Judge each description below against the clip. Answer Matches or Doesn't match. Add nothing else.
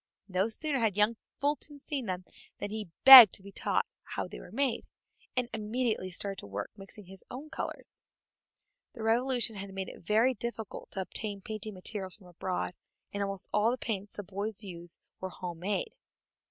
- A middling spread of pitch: Matches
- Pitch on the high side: Matches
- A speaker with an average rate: Matches